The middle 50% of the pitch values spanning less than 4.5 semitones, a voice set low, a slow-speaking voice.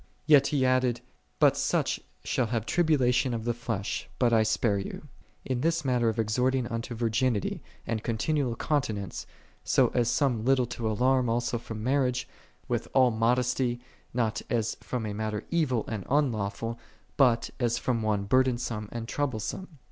No: narrow, 2.5 semitones; low, 120 Hz; average, 165 wpm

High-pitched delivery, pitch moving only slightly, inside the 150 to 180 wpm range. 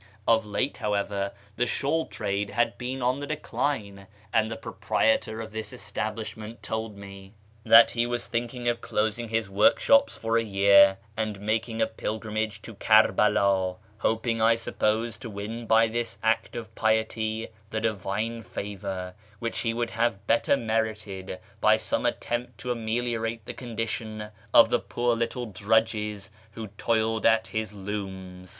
No: low, 110 Hz; narrow, 2.0 semitones; average, 155 wpm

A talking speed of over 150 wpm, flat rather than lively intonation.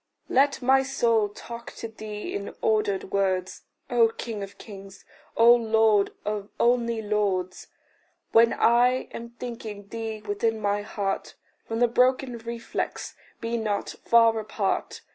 No: slow, 135 wpm; narrow, 2.3 semitones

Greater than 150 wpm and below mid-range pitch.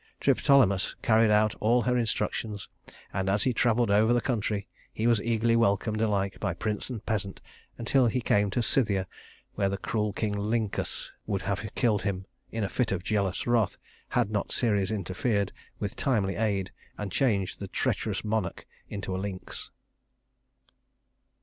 Yes: average, 160 wpm; low, 105 Hz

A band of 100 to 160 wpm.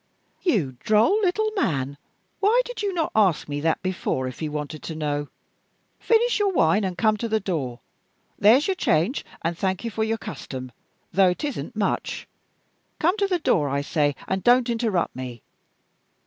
No: average, 175 wpm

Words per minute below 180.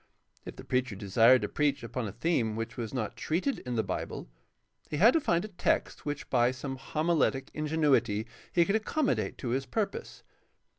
No: average, 185 wpm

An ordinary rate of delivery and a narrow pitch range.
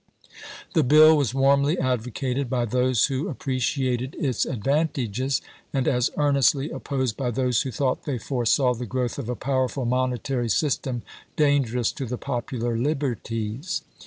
Yes: average, 150 wpm; narrow, 2.3 semitones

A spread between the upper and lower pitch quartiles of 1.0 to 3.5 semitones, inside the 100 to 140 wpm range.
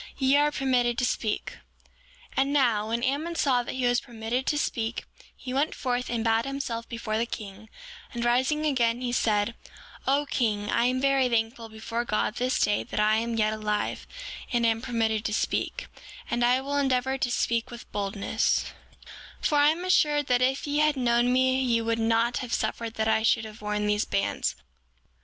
No: average, 2.9 semitones; average, 195 wpm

